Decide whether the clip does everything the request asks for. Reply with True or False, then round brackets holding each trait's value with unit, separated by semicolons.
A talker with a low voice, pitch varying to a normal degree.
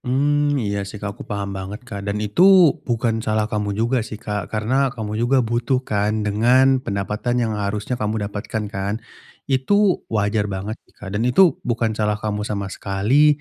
True (110 Hz; 3.5 semitones)